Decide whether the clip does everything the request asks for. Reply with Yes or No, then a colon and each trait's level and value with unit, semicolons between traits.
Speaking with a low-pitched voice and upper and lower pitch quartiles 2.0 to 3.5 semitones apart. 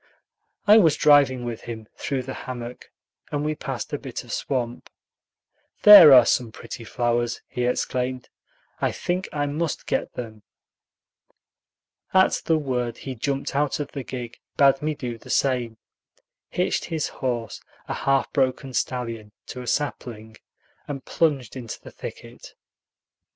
Yes: low, 130 Hz; average, 3.2 semitones